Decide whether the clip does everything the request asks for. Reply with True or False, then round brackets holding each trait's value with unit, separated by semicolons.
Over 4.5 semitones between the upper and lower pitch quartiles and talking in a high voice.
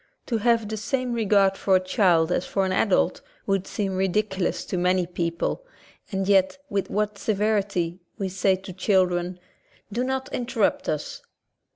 False (2.5 semitones; 195 Hz)